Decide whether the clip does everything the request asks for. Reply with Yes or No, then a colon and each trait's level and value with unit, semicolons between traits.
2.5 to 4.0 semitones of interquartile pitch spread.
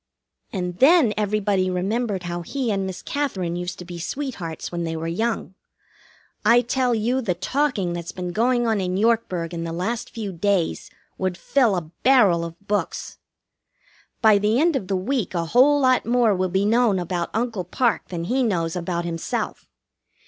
No: average, 5.2 semitones